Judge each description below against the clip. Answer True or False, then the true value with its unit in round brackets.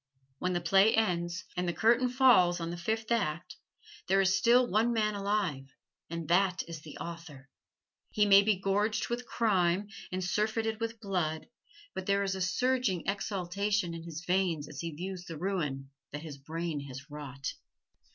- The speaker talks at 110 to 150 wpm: False (170 wpm)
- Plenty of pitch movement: False (4.0 semitones)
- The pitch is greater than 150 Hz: True (185 Hz)